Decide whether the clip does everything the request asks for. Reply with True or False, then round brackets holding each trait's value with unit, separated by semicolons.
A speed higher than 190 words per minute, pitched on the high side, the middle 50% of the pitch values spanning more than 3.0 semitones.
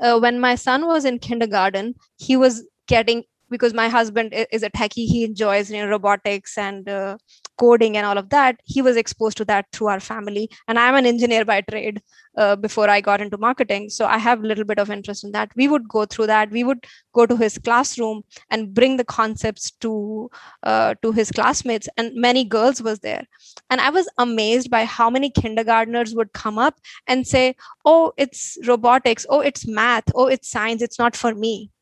False (205 wpm; 230 Hz; 2.5 semitones)